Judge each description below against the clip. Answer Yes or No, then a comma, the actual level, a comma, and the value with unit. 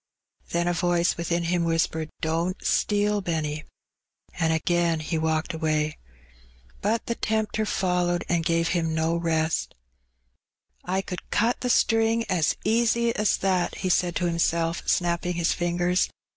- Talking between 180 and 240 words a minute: No, average, 170 wpm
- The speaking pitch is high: No, medium, 175 Hz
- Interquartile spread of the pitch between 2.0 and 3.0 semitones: Yes, narrow, 2.5 semitones